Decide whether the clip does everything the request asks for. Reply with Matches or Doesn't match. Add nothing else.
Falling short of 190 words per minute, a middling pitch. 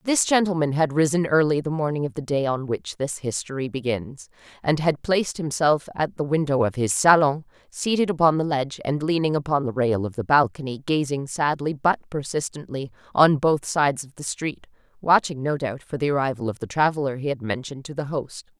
Doesn't match